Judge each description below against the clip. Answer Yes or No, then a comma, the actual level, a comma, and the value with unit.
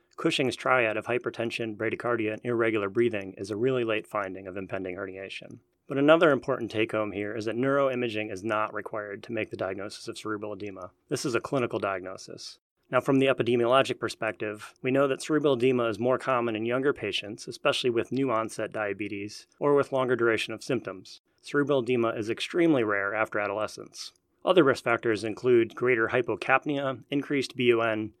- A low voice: Yes, low, 115 Hz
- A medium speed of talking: Yes, average, 175 wpm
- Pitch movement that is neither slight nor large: Yes, average, 3.3 semitones